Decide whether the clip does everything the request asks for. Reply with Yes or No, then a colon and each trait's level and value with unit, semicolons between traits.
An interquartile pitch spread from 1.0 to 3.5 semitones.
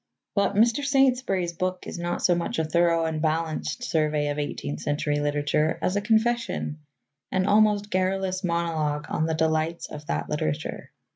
No: average, 4.4 semitones